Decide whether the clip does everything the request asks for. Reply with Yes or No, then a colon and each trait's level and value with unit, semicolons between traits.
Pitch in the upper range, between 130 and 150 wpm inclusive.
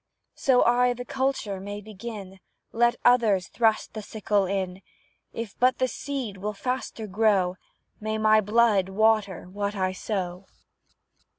Yes: high, 215 Hz; slow, 135 wpm